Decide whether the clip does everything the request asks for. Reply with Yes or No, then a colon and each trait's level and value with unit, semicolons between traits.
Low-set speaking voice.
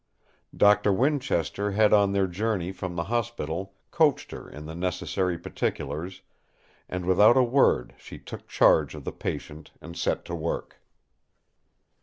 Yes: very low, 95 Hz